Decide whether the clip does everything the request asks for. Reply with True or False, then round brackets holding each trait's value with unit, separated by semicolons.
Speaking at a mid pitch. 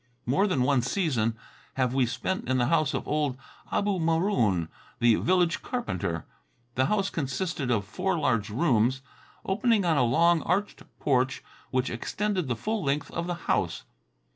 True (145 Hz)